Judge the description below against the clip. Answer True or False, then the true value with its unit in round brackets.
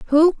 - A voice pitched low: False (320 Hz)